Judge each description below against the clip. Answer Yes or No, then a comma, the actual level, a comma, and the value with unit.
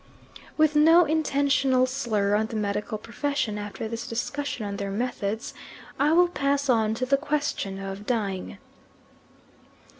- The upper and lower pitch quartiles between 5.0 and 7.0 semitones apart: Yes, wide, 5.4 semitones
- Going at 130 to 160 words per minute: Yes, average, 140 wpm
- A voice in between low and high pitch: No, high, 240 Hz